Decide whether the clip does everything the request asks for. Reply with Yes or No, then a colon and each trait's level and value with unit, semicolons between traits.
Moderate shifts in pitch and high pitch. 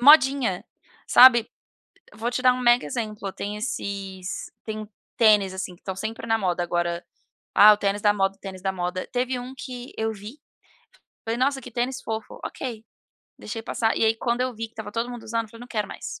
Yes: average, 3.5 semitones; high, 220 Hz